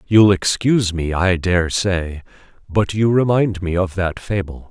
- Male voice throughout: Yes, male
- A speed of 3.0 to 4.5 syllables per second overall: Yes, 4.1 syllables/s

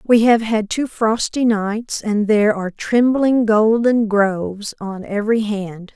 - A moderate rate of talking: Yes, average, 150 wpm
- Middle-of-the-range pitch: No, high, 215 Hz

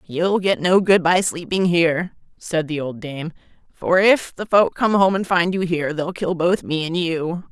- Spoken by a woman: No, male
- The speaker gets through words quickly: Yes, fast, 215 wpm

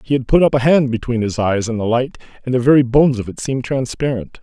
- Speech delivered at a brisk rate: Yes, fast, 270 wpm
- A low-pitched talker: Yes, low, 125 Hz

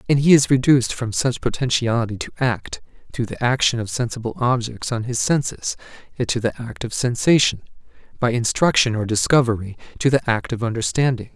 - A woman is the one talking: No, male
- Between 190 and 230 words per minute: No, average, 160 wpm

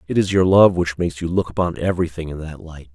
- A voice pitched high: No, very low, 85 Hz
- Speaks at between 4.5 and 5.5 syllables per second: No, 6.5 syllables/s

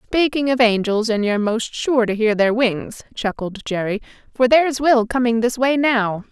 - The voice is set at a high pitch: Yes, high, 235 Hz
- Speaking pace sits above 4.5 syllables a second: Yes, 4.8 syllables/s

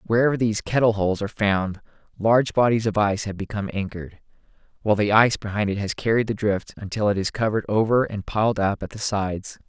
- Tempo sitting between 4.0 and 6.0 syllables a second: No, 6.6 syllables/s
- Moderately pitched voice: No, low, 105 Hz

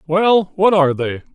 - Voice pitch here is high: No, medium, 175 Hz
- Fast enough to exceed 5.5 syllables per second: No, 4.8 syllables/s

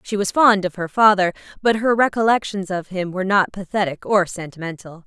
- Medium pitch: No, high, 195 Hz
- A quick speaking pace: No, average, 190 wpm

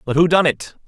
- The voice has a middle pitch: Yes, medium, 150 Hz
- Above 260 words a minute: Yes, fast, 275 wpm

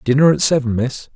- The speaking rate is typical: No, fast, 210 wpm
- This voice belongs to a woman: No, male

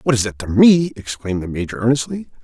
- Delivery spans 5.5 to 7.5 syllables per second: Yes, 6.4 syllables/s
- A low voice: Yes, low, 120 Hz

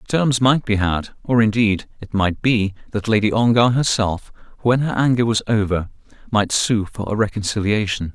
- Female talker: No, male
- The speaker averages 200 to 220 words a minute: No, average, 170 wpm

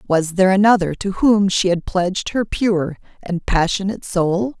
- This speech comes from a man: No, female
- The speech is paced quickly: No, average, 170 wpm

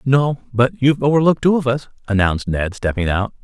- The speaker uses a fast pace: No, average, 190 wpm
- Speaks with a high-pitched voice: No, low, 125 Hz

